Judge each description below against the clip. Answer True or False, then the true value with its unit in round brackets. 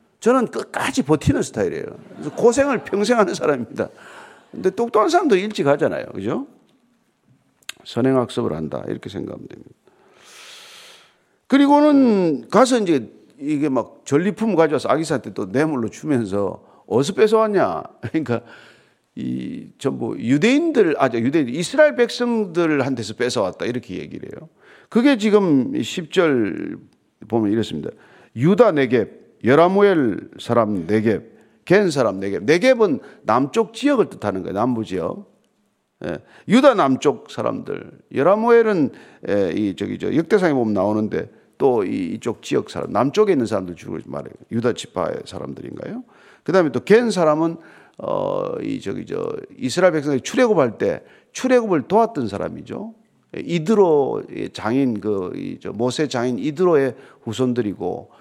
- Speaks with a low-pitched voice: False (210 Hz)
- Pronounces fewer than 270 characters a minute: False (305 characters per minute)